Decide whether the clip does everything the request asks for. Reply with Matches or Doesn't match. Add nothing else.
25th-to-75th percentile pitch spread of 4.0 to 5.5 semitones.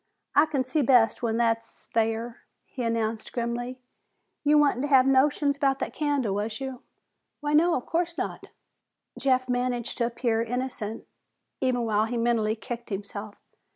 Doesn't match